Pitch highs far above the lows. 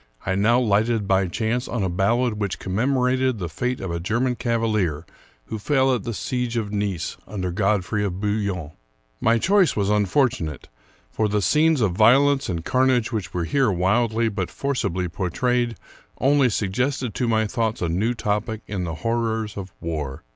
No: average, 4.4 semitones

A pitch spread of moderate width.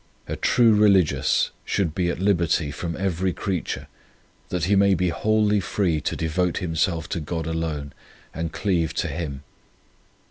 Yes: average, 3.1 semitones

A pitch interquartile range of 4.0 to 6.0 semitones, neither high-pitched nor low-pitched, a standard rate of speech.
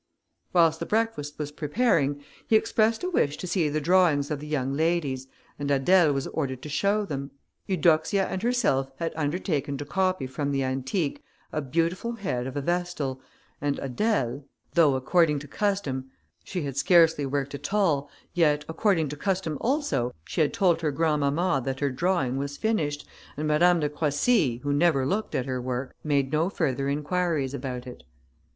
Yes: average, 4.4 semitones; medium, 150 Hz; average, 175 wpm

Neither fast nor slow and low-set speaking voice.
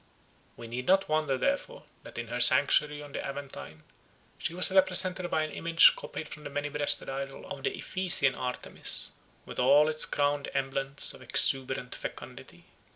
No: average, 165 wpm; medium, 145 Hz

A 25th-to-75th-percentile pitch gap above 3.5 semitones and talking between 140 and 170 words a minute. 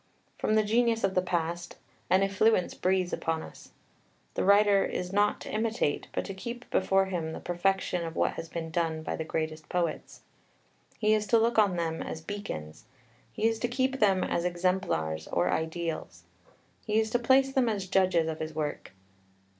No: average, 4.8 semitones; average, 185 wpm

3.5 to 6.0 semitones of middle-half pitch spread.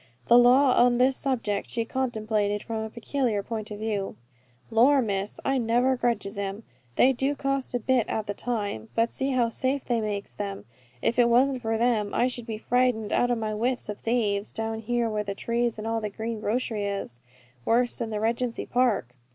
No: average, 2.7 semitones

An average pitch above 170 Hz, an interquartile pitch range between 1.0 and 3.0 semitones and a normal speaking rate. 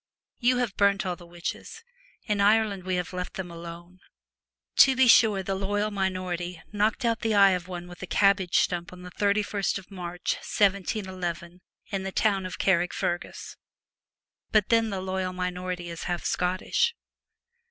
Yes: high, 190 Hz; narrow, 2.4 semitones; average, 175 wpm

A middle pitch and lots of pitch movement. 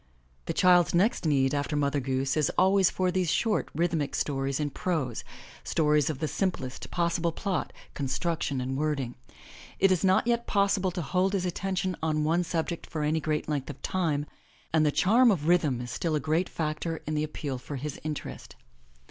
No: medium, 155 Hz; average, 3.9 semitones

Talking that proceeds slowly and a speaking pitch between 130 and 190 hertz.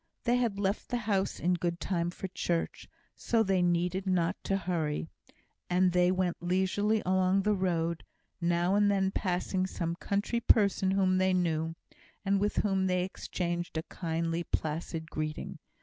No: average, 160 wpm; medium, 185 Hz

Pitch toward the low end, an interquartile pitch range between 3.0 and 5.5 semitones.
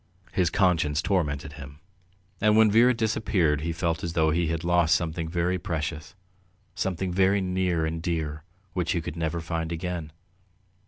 No: very low, 85 Hz; narrow, 2.5 semitones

